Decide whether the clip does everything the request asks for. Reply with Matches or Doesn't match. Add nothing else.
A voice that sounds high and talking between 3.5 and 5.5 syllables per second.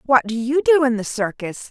Matches